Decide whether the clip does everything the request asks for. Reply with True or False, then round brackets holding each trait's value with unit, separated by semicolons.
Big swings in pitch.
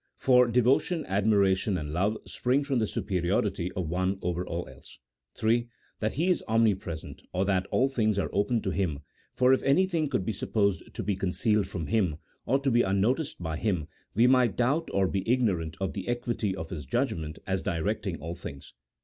False (5.0 semitones)